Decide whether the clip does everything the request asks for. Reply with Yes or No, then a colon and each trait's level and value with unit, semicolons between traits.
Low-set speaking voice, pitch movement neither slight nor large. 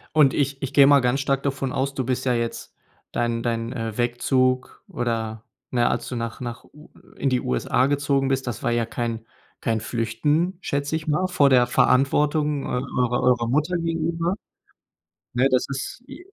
Yes: low, 130 Hz; average, 3.2 semitones